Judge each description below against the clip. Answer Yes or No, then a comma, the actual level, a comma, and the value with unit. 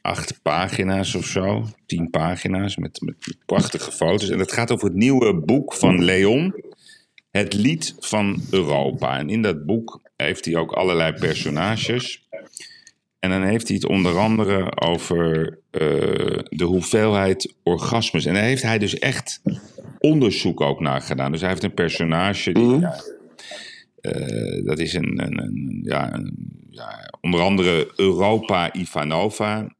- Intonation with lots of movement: No, average, 3.7 semitones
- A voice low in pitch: Yes, very low, 95 Hz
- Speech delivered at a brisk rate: No, average, 145 wpm